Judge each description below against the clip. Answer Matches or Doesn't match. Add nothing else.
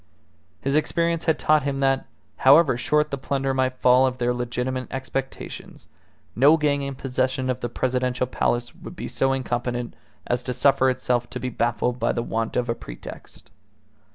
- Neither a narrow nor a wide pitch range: Doesn't match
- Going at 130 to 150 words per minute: Doesn't match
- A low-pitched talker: Matches